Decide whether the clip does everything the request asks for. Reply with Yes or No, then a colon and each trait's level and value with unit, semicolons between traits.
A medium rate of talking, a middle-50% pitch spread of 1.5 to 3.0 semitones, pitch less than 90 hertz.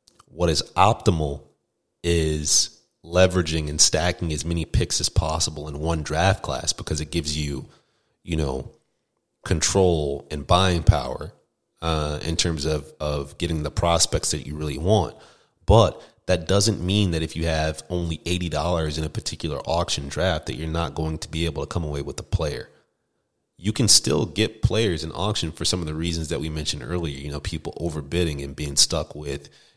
Yes: average, 185 wpm; narrow, 2.6 semitones; very low, 80 Hz